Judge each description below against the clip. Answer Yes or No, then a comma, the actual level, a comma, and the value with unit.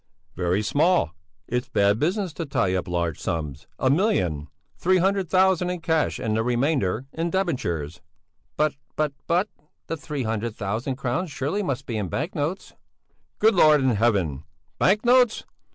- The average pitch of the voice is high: No, low, 135 Hz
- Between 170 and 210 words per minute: No, average, 160 wpm